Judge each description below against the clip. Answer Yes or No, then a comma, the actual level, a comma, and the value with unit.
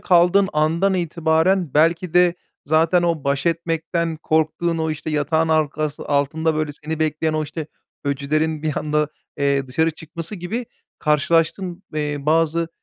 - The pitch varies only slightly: Yes, narrow, 1.8 semitones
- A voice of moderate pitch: Yes, medium, 160 Hz